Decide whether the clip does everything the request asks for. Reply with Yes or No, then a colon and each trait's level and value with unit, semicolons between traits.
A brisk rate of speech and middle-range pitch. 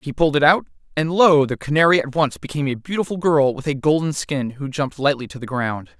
Yes: fast, 240 wpm; medium, 145 Hz